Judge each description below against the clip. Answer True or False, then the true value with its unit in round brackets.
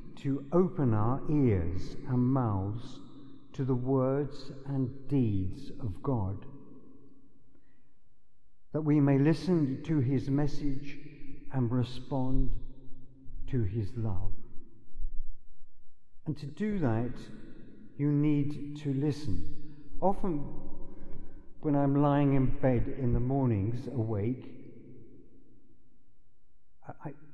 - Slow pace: True (100 wpm)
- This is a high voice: False (135 Hz)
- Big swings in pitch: False (2.8 semitones)